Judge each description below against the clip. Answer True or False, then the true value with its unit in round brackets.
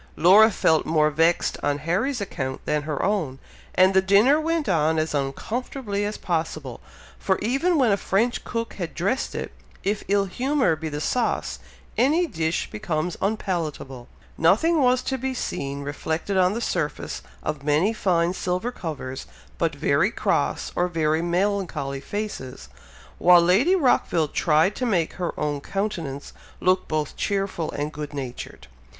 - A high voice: False (180 Hz)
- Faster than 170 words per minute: False (155 wpm)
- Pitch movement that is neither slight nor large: False (5.7 semitones)